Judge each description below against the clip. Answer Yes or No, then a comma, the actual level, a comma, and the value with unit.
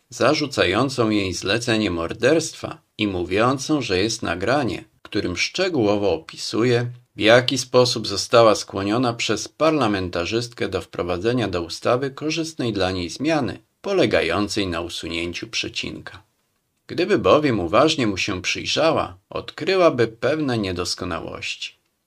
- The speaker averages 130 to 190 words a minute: No, slow, 110 wpm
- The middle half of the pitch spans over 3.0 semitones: Yes, wide, 5.4 semitones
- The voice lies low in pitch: Yes, low, 115 Hz